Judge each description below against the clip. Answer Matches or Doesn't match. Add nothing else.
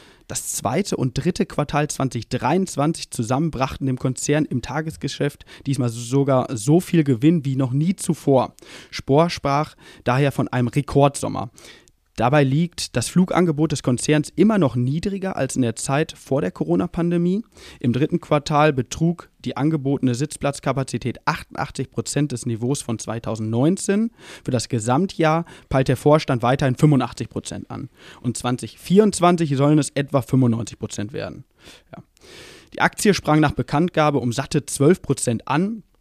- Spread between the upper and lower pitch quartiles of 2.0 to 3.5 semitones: Doesn't match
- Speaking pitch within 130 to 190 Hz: Matches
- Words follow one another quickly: Doesn't match